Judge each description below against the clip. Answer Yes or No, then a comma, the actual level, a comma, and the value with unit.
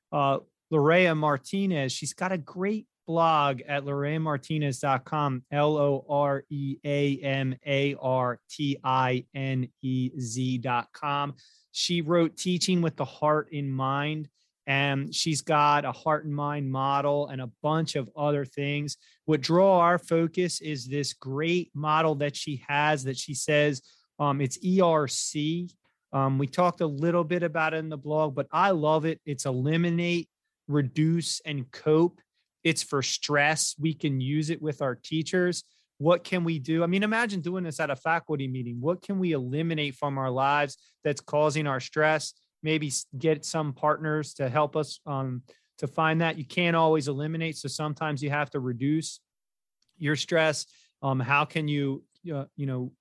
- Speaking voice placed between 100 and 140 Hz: No, medium, 150 Hz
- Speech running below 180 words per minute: Yes, average, 165 wpm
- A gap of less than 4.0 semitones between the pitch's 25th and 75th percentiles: Yes, narrow, 2.5 semitones